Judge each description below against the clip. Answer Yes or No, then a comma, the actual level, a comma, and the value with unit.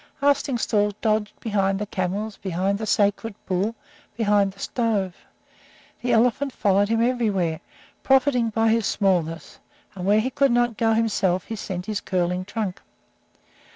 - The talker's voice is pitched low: No, high, 210 Hz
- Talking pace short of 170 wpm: Yes, average, 145 wpm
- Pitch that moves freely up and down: No, average, 3.0 semitones